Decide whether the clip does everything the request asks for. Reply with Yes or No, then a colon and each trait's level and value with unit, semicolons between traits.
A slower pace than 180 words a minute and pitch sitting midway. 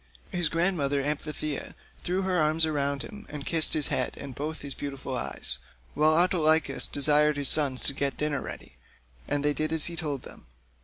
No: average, 185 wpm; medium, 150 Hz